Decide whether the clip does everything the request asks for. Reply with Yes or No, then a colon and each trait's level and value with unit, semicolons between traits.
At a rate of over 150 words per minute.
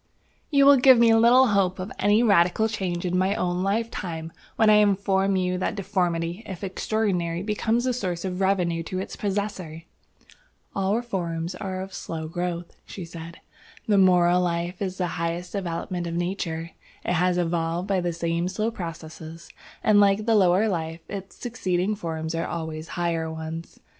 Yes: average, 170 wpm